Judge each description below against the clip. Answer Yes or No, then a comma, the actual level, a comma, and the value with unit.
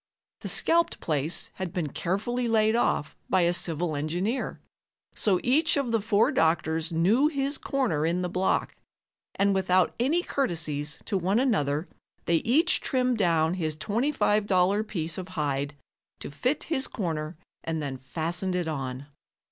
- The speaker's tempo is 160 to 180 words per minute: No, average, 150 wpm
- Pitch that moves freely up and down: Yes, wide, 6.4 semitones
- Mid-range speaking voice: Yes, medium, 180 Hz